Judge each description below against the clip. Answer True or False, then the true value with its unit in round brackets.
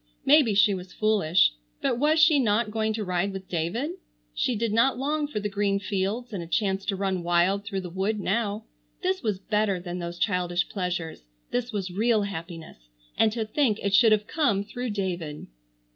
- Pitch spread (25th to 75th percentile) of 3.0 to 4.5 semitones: True (3.5 semitones)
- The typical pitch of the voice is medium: False (205 Hz)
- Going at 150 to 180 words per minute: False (190 wpm)